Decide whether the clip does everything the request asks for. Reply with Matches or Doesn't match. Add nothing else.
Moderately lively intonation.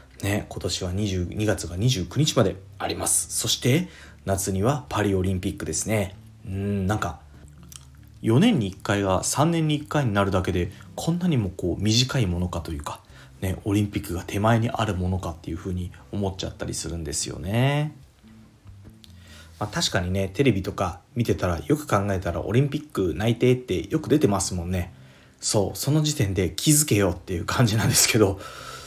Matches